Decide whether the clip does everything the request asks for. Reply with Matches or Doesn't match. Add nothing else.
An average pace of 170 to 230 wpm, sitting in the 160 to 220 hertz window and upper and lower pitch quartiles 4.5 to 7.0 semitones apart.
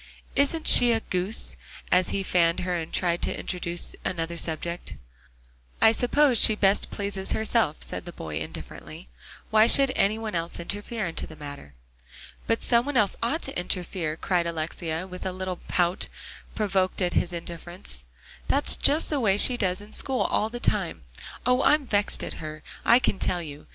Matches